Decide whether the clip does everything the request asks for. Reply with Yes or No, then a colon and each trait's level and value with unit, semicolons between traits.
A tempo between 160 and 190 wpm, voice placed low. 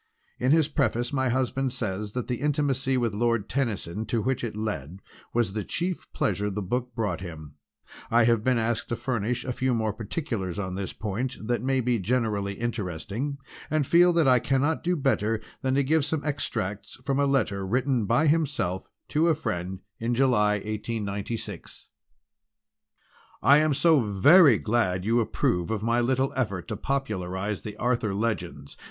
Yes: average, 170 wpm; low, 120 Hz